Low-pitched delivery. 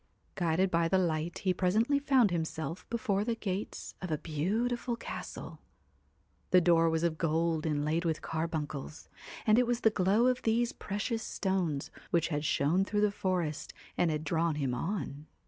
No: medium, 175 Hz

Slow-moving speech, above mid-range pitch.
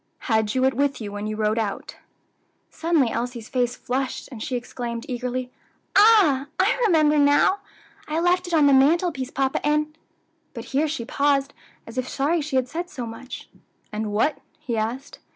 No: average, 180 wpm; very high, 265 Hz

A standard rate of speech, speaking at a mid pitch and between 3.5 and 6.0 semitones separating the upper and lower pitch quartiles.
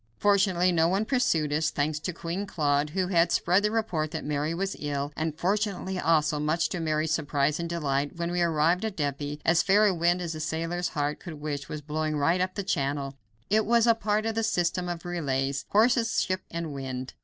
No: fast, 210 wpm; medium, 165 Hz; average, 3.9 semitones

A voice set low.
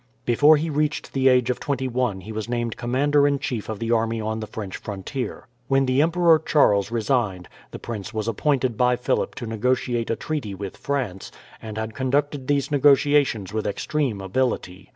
Yes: low, 125 Hz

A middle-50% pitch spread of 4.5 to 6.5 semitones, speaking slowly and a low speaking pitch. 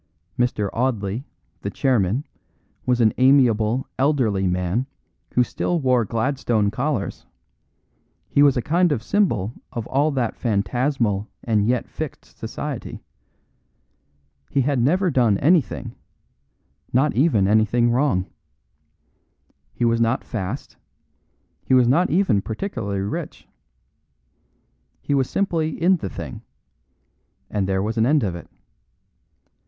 Yes: average, 5.0 semitones; slow, 120 wpm; low, 120 Hz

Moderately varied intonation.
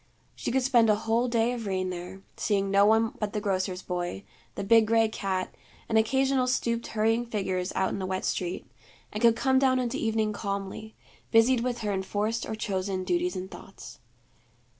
Yes: average, 3.4 semitones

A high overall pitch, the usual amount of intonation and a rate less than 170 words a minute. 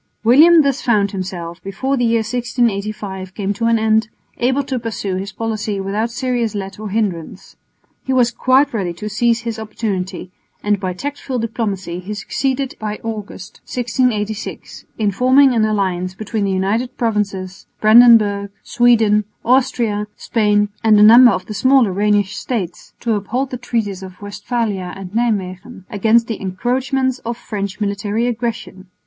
Yes: high, 215 Hz; average, 3.3 semitones; average, 155 wpm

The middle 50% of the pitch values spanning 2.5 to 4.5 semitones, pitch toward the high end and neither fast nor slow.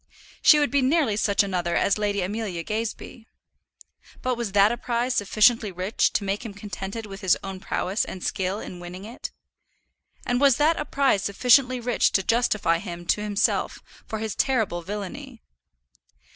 Yes: average, 3.9 semitones; high, 210 Hz; average, 170 wpm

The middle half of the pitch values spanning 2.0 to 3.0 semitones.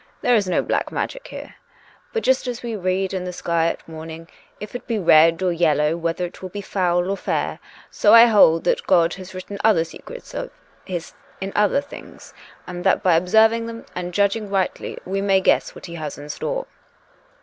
No: average, 3.9 semitones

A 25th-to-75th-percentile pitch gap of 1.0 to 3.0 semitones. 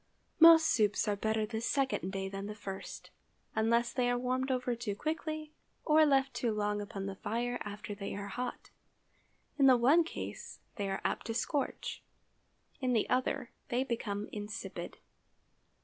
No: average, 4.1 semitones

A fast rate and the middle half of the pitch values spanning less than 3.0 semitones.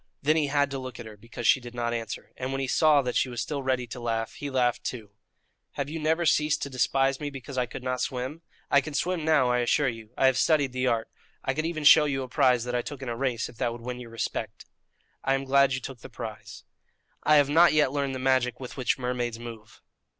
Yes: fast, 260 wpm; narrow, 2.6 semitones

